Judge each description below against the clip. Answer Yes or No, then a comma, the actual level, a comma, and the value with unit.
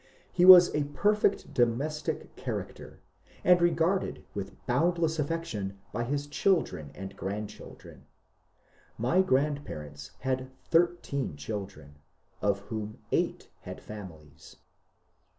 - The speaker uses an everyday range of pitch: No, wide, 8.8 semitones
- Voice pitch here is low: Yes, low, 130 Hz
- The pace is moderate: No, slow, 105 wpm